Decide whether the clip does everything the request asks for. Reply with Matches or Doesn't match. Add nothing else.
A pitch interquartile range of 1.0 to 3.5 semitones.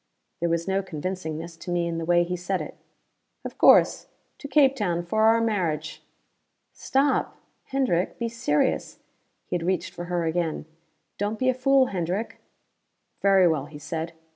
Doesn't match